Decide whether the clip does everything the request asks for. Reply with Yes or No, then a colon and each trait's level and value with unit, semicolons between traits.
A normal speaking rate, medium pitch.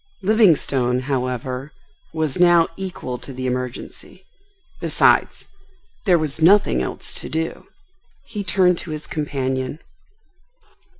No: slow, 110 wpm; medium, 150 Hz